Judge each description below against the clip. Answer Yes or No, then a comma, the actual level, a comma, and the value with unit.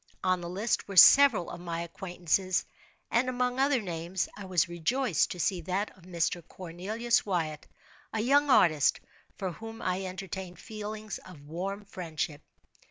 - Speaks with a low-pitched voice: No, medium, 185 Hz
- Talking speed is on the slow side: No, average, 155 wpm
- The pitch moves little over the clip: No, average, 4.0 semitones